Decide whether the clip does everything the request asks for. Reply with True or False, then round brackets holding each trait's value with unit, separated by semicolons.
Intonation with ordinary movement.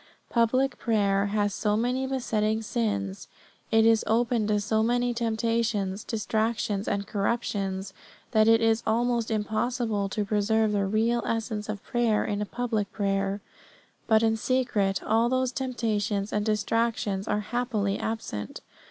False (2.3 semitones)